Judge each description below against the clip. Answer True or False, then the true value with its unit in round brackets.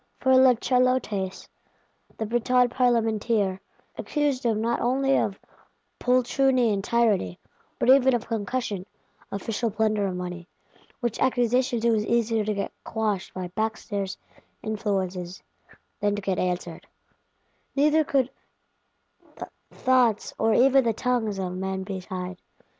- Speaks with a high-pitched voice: True (220 Hz)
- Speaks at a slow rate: True (130 wpm)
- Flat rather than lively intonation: False (4.3 semitones)